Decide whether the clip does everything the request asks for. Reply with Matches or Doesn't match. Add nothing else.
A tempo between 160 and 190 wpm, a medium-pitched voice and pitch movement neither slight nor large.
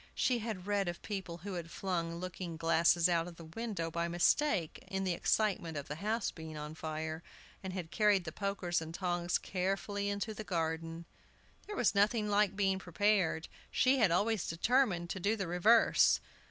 Matches